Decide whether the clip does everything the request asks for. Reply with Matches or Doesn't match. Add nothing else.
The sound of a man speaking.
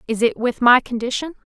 Doesn't match